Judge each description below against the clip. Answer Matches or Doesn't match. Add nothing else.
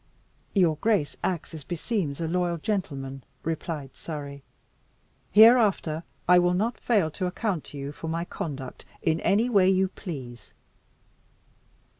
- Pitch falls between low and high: Matches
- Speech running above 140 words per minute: Doesn't match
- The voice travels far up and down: Doesn't match